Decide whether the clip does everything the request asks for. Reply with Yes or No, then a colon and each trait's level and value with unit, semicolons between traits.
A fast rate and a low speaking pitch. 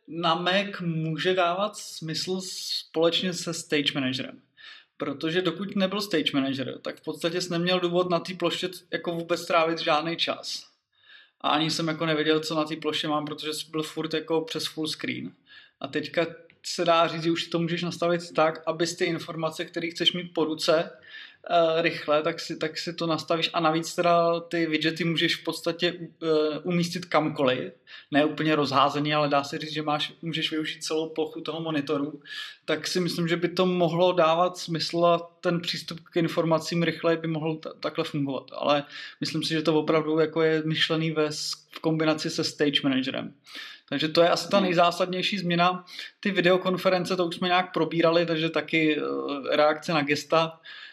No: fast, 180 wpm; medium, 165 Hz